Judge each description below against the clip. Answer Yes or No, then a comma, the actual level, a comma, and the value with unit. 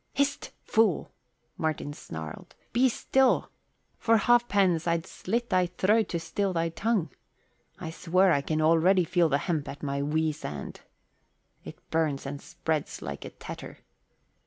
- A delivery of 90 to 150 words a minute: Yes, average, 140 wpm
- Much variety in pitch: No, average, 4.5 semitones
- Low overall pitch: No, medium, 170 Hz